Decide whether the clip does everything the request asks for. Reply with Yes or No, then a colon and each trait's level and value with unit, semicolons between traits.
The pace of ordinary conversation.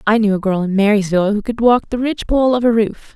No: fast, 265 wpm